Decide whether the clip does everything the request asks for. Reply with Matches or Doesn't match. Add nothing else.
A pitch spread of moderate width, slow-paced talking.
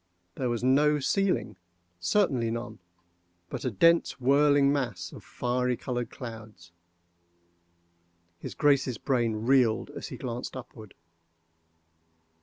Doesn't match